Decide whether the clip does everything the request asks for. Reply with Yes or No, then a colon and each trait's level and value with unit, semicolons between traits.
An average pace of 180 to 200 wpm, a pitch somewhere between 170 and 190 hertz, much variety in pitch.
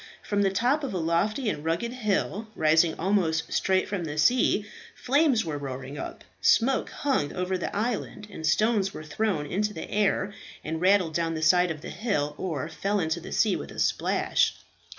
No: average, 190 wpm; medium, 185 Hz; average, 4.8 semitones